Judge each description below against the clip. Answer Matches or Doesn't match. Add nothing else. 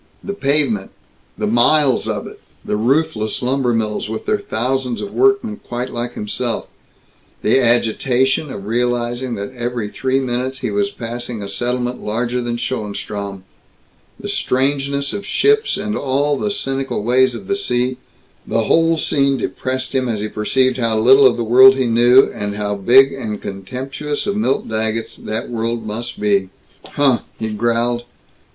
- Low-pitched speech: Matches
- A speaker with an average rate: Matches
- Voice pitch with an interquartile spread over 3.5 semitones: Doesn't match